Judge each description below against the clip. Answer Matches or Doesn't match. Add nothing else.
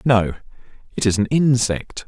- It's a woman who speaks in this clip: Doesn't match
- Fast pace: Doesn't match